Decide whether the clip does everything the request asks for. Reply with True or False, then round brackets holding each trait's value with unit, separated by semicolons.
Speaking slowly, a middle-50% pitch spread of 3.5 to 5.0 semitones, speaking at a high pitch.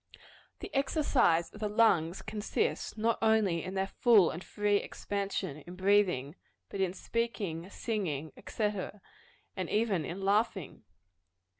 True (130 wpm; 4.0 semitones; 200 Hz)